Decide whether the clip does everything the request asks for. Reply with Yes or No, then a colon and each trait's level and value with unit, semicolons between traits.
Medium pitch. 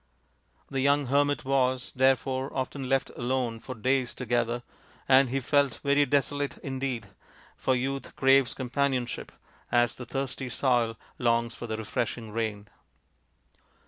No: low, 130 Hz